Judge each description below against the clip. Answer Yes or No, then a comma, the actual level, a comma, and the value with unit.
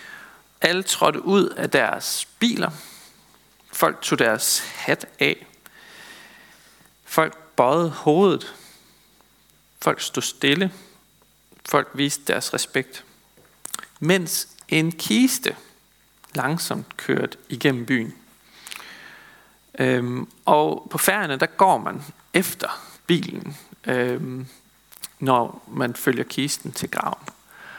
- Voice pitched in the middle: Yes, medium, 165 Hz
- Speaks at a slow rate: Yes, slow, 95 wpm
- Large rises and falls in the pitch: Yes, wide, 6.7 semitones